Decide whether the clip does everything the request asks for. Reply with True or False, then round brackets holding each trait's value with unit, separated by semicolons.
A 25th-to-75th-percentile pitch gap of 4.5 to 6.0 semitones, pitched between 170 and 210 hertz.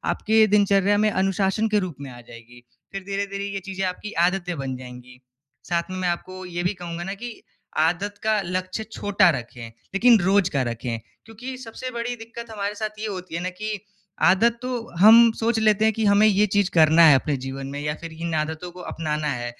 True (4.8 semitones; 190 Hz)